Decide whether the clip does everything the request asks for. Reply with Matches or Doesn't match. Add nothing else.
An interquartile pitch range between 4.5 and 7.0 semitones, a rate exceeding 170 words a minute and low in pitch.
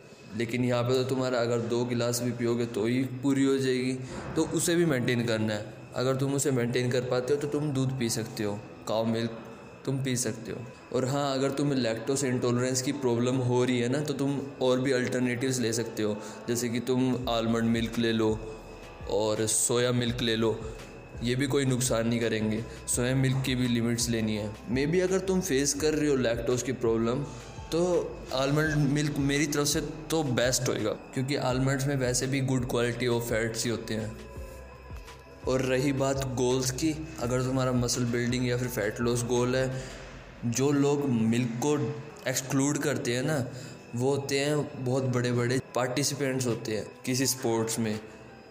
Doesn't match